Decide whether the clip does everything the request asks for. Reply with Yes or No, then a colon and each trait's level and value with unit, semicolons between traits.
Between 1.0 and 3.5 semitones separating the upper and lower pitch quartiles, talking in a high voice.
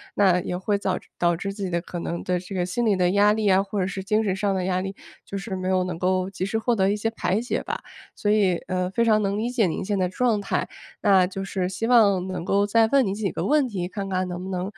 Yes: narrow, 2.4 semitones; high, 195 Hz